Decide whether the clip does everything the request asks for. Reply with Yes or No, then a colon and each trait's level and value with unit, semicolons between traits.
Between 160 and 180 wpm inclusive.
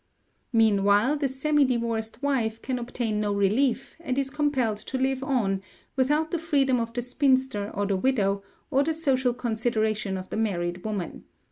Yes: average, 165 wpm